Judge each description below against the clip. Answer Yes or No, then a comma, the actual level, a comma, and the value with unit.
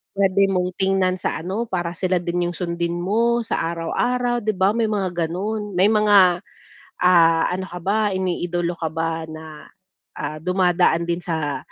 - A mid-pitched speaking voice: Yes, medium, 180 Hz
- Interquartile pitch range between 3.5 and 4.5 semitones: No, narrow, 2.6 semitones